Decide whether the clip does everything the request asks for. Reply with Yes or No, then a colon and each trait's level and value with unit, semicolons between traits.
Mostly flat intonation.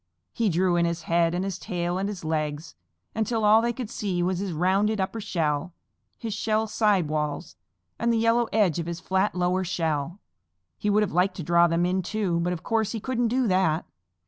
No: average, 3.9 semitones